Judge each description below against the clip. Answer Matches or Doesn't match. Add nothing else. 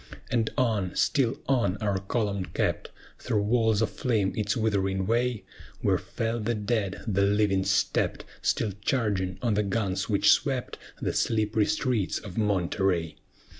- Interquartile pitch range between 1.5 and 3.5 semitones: Matches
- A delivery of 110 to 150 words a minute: Matches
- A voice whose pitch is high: Doesn't match